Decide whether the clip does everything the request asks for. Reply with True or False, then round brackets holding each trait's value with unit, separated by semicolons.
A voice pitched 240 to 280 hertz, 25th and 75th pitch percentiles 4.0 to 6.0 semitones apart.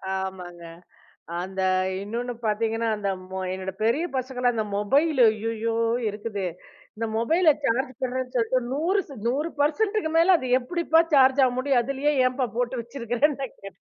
True (245 Hz; 4.3 semitones)